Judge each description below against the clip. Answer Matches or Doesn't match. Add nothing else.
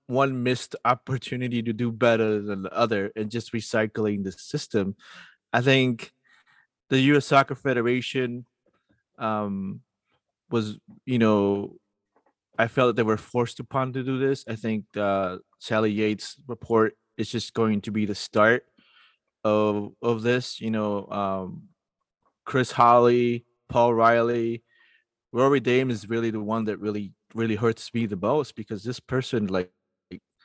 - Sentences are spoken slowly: Doesn't match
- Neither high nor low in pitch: Doesn't match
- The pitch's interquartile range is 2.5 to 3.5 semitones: Matches